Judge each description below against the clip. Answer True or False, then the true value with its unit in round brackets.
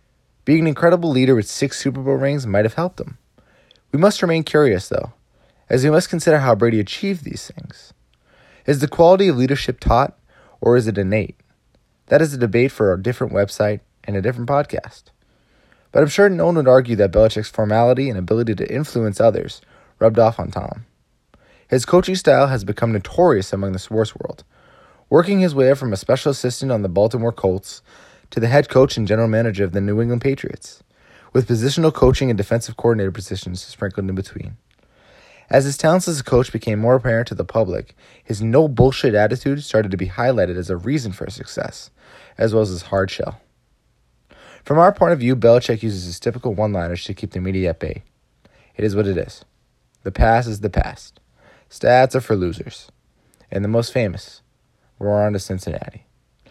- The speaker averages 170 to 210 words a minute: True (195 wpm)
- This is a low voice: True (115 Hz)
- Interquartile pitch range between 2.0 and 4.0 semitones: False (4.6 semitones)